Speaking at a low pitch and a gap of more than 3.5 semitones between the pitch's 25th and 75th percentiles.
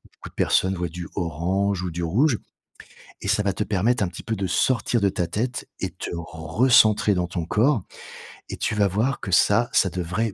Yes: low, 100 Hz; average, 4.0 semitones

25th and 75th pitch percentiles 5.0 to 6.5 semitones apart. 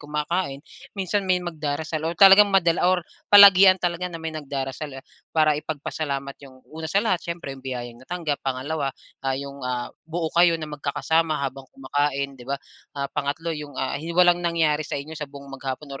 No: average, 3.5 semitones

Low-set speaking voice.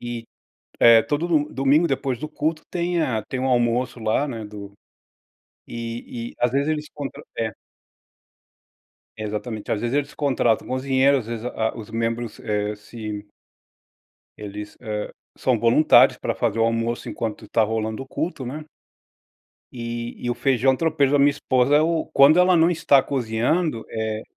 Yes: low, 120 Hz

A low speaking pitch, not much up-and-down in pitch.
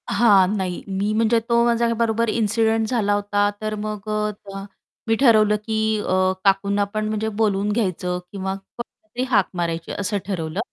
No: high, 210 Hz; narrow, 2.0 semitones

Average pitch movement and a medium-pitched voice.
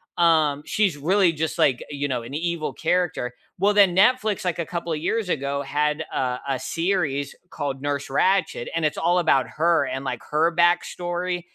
Yes: average, 3.9 semitones; medium, 165 Hz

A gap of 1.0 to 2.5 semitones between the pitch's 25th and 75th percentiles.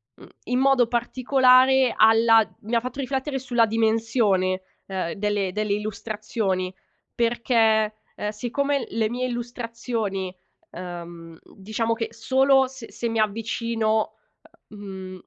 No: average, 2.9 semitones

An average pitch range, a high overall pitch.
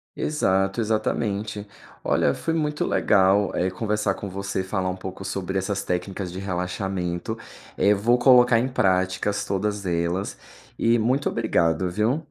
No: average, 3.0 semitones; low, 100 Hz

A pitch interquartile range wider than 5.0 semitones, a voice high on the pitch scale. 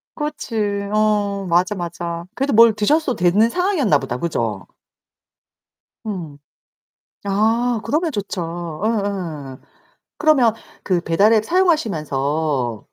Yes: wide, 5.5 semitones; high, 200 Hz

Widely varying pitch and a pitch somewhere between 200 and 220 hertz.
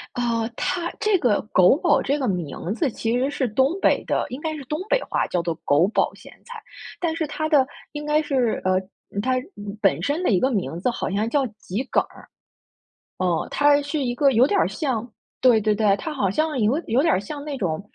No: wide, 6.2 semitones; very high, 255 Hz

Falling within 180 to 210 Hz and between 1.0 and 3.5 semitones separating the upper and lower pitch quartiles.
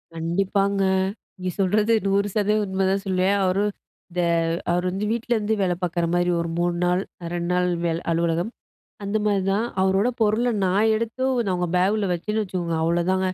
Yes: high, 190 Hz; average, 2.9 semitones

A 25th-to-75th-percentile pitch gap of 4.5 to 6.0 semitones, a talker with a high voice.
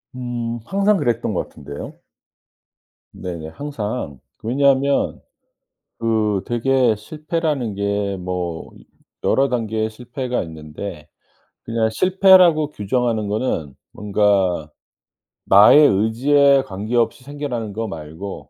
No: average, 5.2 semitones; low, 115 Hz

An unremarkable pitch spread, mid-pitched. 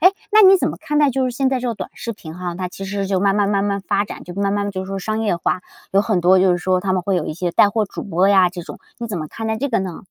No: average, 3.2 semitones; high, 195 Hz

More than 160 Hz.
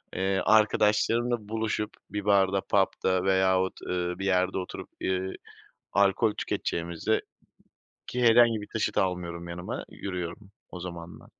No: very low, 95 Hz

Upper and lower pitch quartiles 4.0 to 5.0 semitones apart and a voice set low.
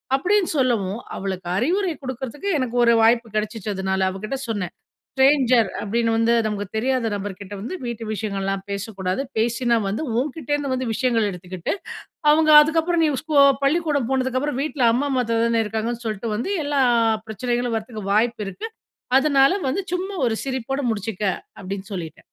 No: average, 4.4 semitones; high, 235 Hz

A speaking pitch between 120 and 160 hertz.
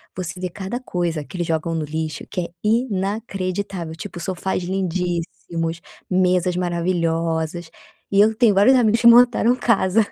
No: medium, 185 Hz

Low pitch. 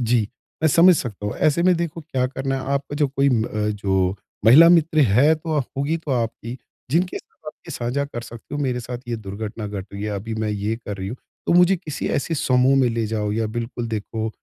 Yes: low, 125 Hz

